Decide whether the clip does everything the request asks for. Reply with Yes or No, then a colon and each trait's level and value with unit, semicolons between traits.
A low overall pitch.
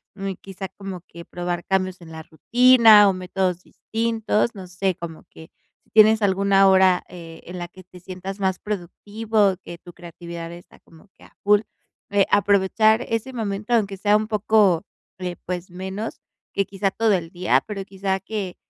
No: high, 195 Hz